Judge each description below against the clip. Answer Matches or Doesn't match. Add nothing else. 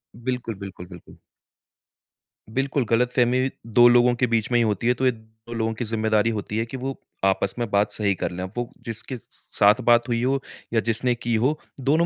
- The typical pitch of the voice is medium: Doesn't match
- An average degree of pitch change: Doesn't match